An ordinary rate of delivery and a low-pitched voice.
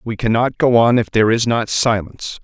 No: fast, 220 wpm; low, 115 Hz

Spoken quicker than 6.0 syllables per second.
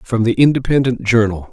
No: 5.4 syllables/s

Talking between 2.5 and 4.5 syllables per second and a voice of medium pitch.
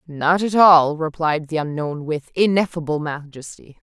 Yes: 4.4 syllables/s; medium, 160 Hz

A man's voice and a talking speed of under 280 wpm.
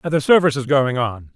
Yes: male; fast, 220 wpm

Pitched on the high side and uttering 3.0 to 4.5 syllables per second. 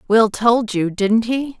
Yes: high, 225 Hz; 3.6 syllables/s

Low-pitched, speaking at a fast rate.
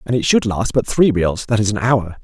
Yes: low, 110 Hz; fast, 295 wpm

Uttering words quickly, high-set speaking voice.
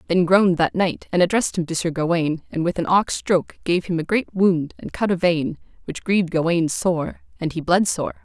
No: fast, 235 wpm; medium, 175 Hz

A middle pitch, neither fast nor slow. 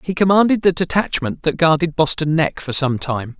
Yes: medium, 155 Hz; average, 195 wpm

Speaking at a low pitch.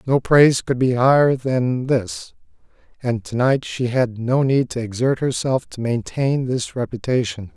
Yes: low, 125 Hz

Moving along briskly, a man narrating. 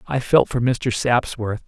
No: average, 180 wpm; male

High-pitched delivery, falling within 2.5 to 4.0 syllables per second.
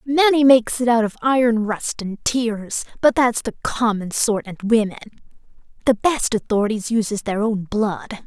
No: high, 225 Hz; 4.8 syllables/s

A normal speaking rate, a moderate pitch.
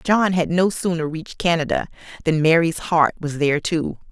Yes: average, 175 wpm; medium, 165 Hz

